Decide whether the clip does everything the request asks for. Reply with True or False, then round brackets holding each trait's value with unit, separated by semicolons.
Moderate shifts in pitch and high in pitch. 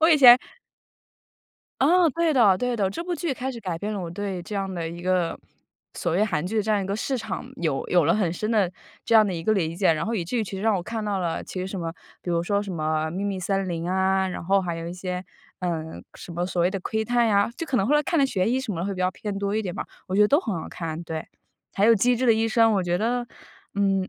True (4.1 semitones; 195 Hz)